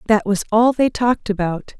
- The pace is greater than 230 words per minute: No, average, 200 wpm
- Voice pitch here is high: Yes, high, 215 Hz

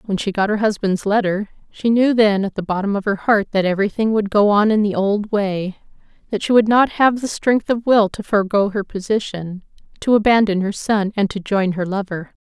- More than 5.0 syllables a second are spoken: Yes, 5.4 syllables/s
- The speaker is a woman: Yes, female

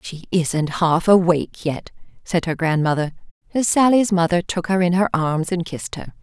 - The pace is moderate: Yes, average, 185 wpm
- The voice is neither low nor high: Yes, medium, 175 Hz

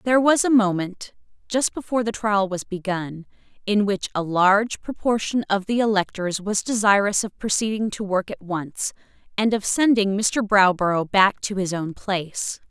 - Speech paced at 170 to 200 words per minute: No, average, 160 wpm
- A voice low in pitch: No, high, 205 Hz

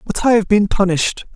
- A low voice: No, high, 200 Hz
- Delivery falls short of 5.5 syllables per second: No, 5.8 syllables/s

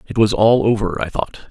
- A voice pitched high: No, low, 105 Hz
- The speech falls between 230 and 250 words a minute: Yes, fast, 240 wpm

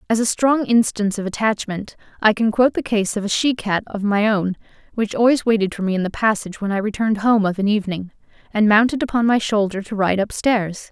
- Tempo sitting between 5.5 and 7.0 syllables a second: Yes, 6.0 syllables/s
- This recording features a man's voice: No, female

